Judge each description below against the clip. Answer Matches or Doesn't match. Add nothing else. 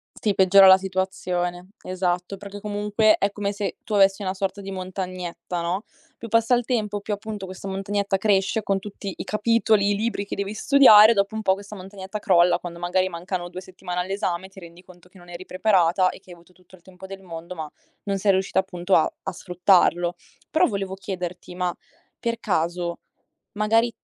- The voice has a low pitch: Doesn't match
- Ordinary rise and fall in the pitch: Doesn't match